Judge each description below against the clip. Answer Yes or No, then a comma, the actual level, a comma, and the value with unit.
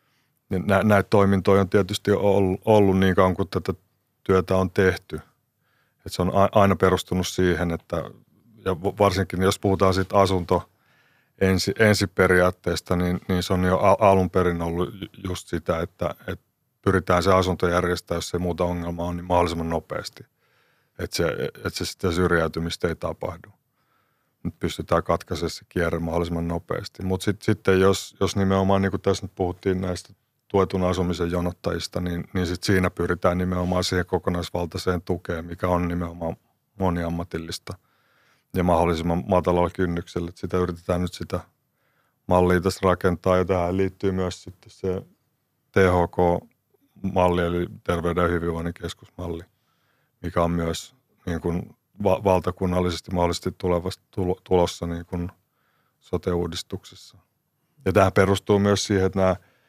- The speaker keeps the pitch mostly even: Yes, narrow, 1.9 semitones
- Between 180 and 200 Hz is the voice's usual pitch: No, very low, 95 Hz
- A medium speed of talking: Yes, average, 140 wpm